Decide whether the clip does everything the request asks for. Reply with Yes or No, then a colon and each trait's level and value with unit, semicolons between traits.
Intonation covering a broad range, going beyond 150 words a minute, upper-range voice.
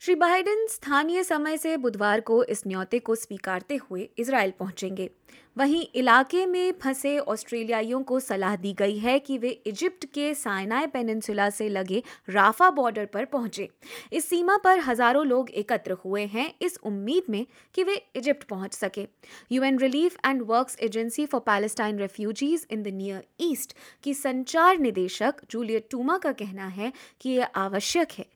Yes: wide, 5.7 semitones; average, 160 wpm; high, 245 Hz